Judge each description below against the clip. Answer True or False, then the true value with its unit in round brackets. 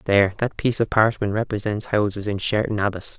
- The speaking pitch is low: True (105 Hz)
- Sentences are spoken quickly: False (190 wpm)